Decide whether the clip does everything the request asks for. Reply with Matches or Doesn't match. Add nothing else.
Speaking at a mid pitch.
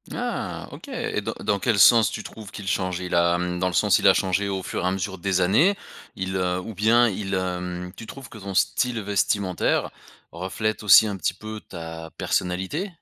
Doesn't match